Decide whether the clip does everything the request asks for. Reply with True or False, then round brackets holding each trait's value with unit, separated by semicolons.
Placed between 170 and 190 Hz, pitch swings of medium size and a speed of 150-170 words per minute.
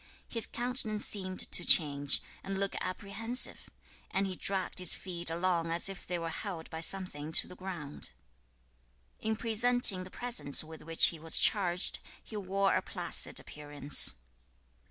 True (185 Hz; 3.5 semitones; 155 wpm)